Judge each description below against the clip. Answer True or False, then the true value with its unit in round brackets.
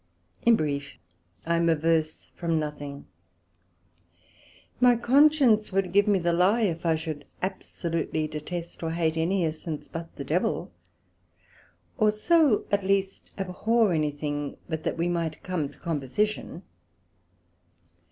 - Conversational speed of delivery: False (130 wpm)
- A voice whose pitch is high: False (170 Hz)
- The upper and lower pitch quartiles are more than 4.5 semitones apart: False (4.2 semitones)